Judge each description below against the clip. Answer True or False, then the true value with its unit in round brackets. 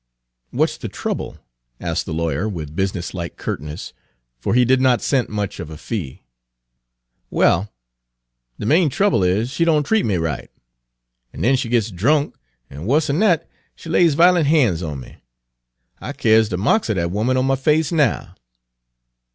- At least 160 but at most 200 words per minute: True (170 wpm)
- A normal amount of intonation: False (8.7 semitones)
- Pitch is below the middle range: True (115 Hz)